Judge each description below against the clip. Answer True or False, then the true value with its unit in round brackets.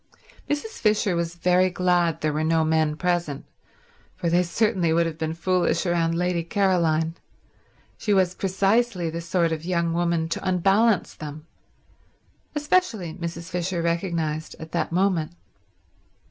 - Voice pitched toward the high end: False (170 Hz)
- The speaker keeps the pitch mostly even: True (2.2 semitones)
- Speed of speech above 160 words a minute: False (140 wpm)